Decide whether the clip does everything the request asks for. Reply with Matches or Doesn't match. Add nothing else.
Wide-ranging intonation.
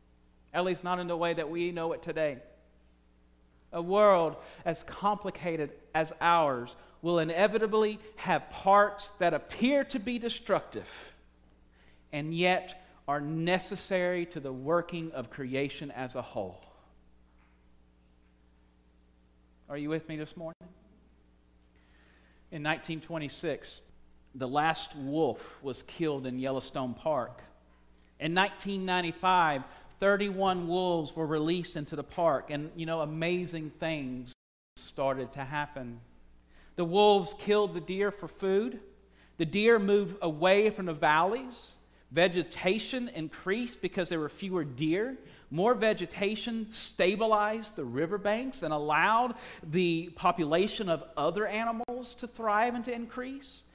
Matches